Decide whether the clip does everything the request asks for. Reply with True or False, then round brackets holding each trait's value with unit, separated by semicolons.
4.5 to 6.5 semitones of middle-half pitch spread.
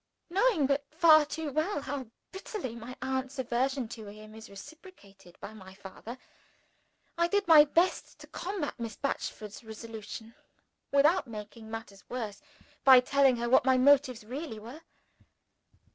True (4.8 semitones)